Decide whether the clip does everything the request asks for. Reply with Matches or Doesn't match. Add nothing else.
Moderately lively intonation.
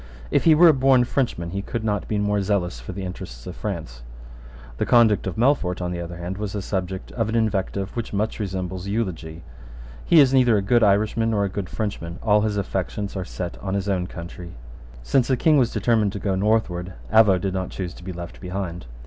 Matches